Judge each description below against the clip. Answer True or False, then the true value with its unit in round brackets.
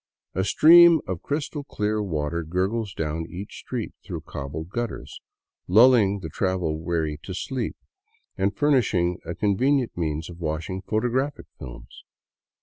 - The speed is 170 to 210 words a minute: False (140 wpm)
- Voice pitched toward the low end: True (95 Hz)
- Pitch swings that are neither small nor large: False (6.4 semitones)